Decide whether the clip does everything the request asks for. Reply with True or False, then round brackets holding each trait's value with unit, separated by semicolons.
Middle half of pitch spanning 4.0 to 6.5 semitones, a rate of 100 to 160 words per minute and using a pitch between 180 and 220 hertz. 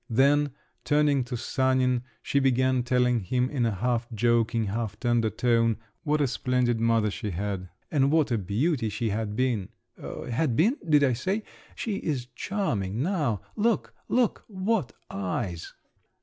False (4.5 semitones; 150 wpm; 125 Hz)